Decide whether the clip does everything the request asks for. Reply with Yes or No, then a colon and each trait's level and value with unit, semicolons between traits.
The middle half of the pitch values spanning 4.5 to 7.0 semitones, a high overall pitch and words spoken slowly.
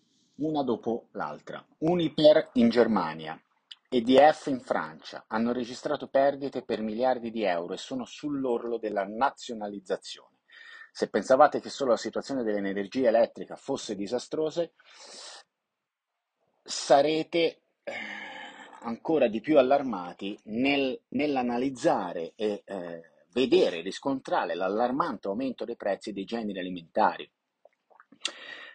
No: average, 4.9 semitones; low, 120 Hz; slow, 105 wpm